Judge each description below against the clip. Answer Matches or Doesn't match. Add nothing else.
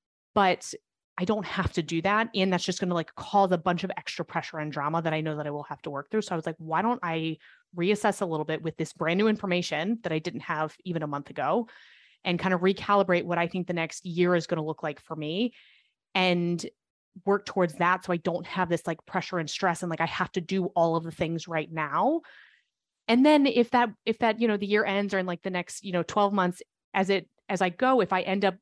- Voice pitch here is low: Doesn't match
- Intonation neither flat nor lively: Matches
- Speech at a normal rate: Doesn't match